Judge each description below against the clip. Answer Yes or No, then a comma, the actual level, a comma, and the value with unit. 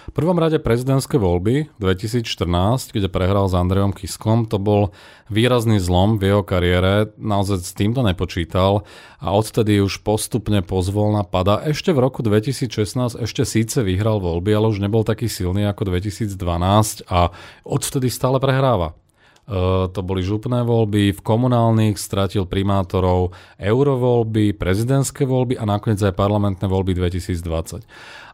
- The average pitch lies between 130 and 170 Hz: No, low, 105 Hz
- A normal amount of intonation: Yes, average, 3.7 semitones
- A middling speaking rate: Yes, average, 140 wpm